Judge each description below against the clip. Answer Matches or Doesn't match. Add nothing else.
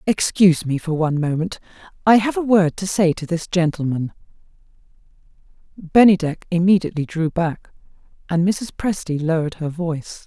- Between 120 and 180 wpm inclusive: Matches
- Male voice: Doesn't match